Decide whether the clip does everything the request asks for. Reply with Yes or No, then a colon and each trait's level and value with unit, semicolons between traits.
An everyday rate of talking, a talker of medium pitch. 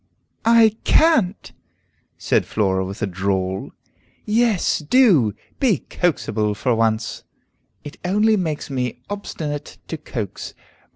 No: slow, 110 wpm; medium, 145 Hz